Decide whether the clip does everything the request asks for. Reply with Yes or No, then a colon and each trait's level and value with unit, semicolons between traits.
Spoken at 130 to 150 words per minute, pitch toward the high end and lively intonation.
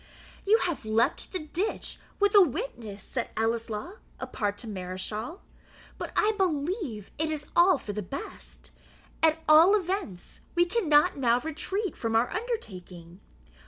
Yes: average, 140 wpm; very high, 295 Hz; wide, 8.9 semitones